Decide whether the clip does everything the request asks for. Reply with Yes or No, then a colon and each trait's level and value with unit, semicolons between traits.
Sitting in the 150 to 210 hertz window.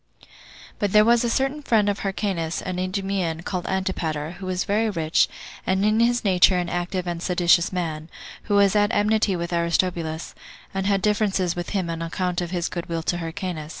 Yes: medium, 185 Hz